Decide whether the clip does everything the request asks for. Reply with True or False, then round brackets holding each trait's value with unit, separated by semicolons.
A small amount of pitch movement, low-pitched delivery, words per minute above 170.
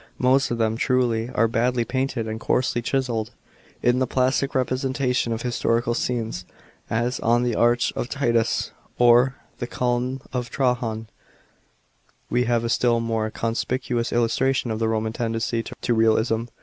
False (1.8 semitones; 120 Hz; 155 wpm)